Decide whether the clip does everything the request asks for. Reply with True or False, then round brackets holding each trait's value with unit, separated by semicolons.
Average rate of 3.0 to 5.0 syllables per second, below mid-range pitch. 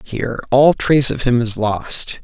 True (4.5 syllables/s; 120 Hz)